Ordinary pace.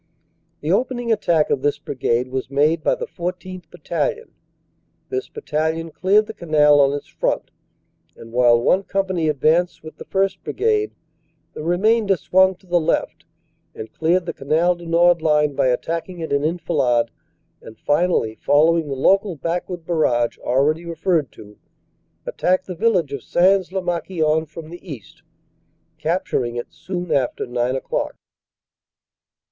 Yes: average, 150 wpm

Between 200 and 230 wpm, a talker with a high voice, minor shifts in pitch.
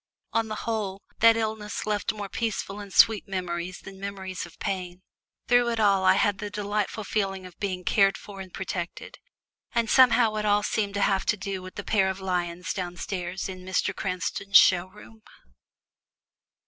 No: average, 175 wpm; high, 195 Hz; narrow, 2.2 semitones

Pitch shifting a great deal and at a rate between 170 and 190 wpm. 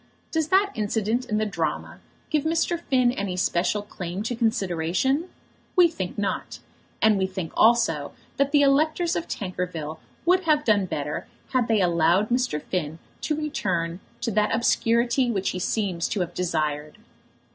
No: wide, 6.9 semitones; average, 155 wpm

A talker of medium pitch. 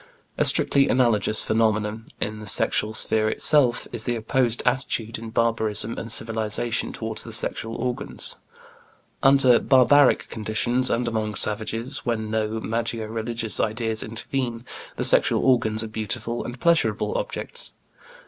No: low, 115 Hz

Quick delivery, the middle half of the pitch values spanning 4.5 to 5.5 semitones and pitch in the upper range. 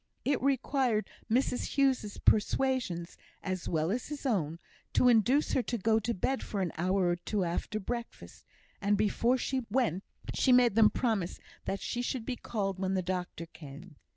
No: average, 175 wpm; average, 5.1 semitones; high, 215 Hz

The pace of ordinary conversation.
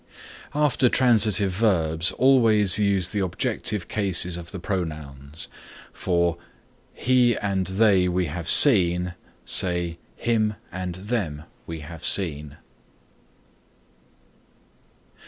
No: slow, 100 wpm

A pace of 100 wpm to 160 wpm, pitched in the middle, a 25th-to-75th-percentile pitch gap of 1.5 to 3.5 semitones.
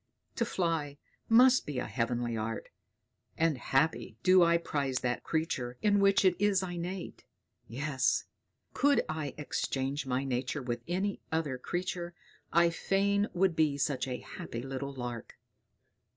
No: average, 140 wpm; medium, 155 Hz; wide, 5.6 semitones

